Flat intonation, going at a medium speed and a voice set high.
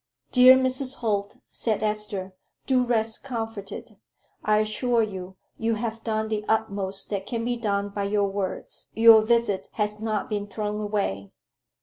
Yes: narrow, 2.2 semitones; average, 150 wpm; high, 215 Hz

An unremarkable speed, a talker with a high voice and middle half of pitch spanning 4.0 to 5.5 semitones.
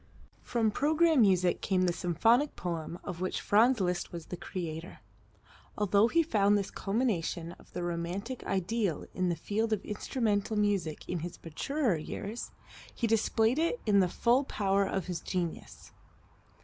Yes: average, 155 wpm; high, 200 Hz; average, 4.4 semitones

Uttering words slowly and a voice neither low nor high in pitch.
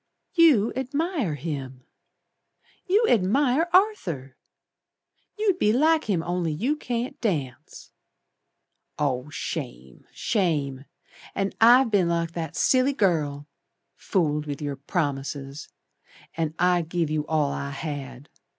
Yes: slow, 115 wpm; medium, 170 Hz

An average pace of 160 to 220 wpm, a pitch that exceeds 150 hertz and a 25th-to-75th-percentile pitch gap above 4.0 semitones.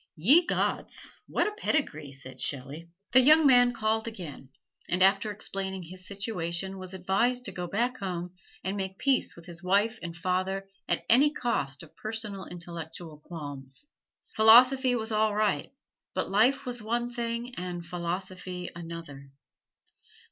No: average, 150 wpm; high, 190 Hz; average, 5.3 semitones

